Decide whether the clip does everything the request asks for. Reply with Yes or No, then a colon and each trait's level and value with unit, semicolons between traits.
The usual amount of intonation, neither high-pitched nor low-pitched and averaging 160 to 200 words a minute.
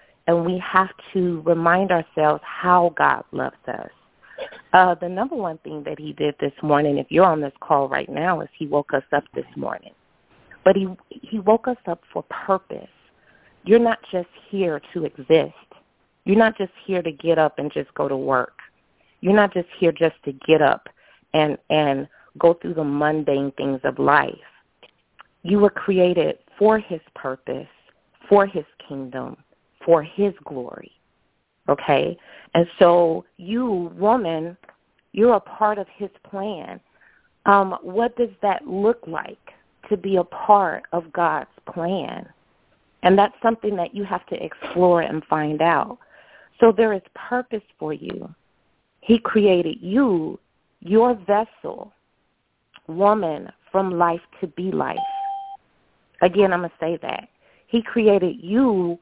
No: average, 4.3 semitones; medium, 180 Hz; average, 150 wpm